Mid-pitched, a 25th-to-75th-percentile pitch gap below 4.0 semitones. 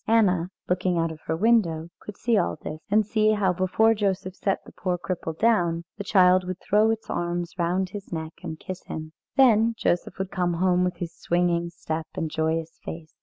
Yes: medium, 180 Hz; average, 3.3 semitones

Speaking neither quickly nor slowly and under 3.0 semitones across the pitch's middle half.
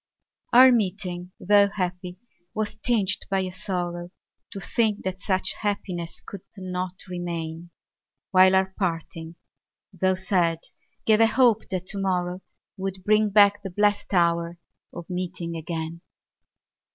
No: slow, 130 wpm; narrow, 2.5 semitones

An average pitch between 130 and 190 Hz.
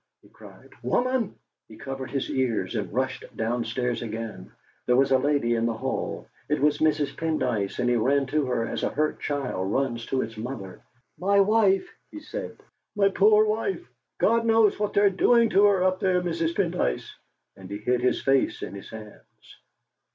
Yes: medium, 140 Hz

